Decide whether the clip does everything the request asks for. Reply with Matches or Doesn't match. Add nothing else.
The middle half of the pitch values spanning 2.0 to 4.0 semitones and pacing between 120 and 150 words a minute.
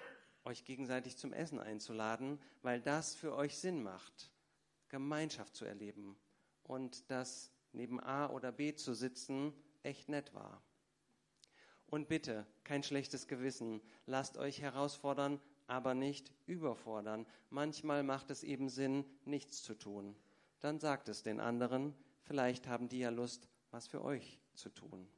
Matches